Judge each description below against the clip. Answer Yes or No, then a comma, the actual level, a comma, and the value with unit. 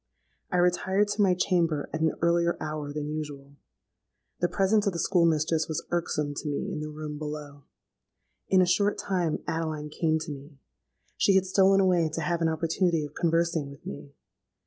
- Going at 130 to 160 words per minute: No, average, 185 wpm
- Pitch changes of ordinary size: Yes, average, 3.0 semitones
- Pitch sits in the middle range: Yes, medium, 160 Hz